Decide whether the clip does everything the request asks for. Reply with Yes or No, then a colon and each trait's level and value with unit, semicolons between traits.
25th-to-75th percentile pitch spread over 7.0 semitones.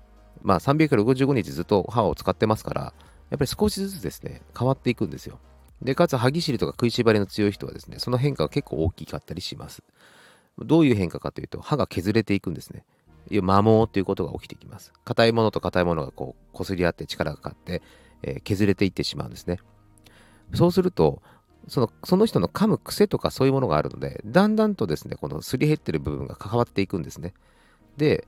No: wide, 6.2 semitones